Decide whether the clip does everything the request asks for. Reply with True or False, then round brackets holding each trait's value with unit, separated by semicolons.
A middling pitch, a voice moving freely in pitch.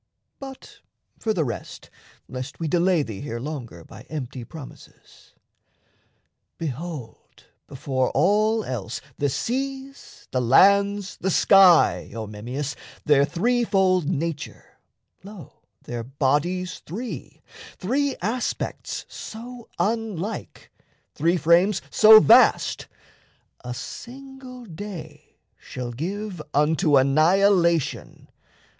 True (170 Hz; 7.2 semitones)